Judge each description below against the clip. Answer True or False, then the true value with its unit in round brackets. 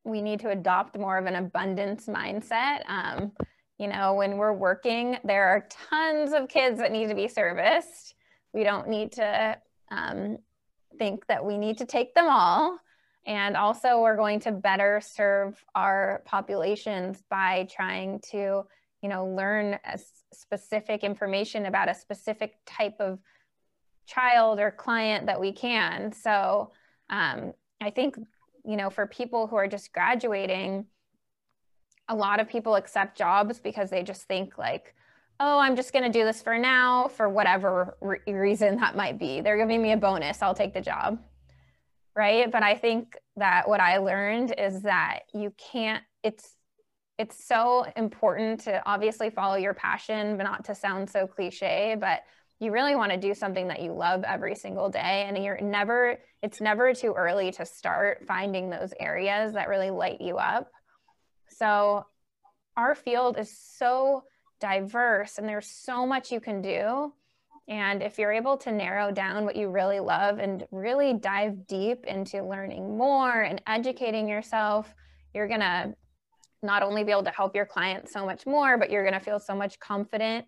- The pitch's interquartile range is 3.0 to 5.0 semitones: False (2.6 semitones)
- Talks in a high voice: True (210 Hz)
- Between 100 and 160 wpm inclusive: False (170 wpm)